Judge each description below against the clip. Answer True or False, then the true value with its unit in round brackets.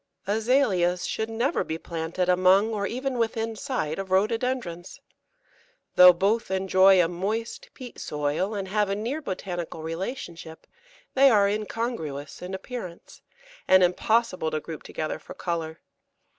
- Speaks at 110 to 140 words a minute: True (135 wpm)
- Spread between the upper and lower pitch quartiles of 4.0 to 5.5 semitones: True (4.6 semitones)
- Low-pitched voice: False (190 Hz)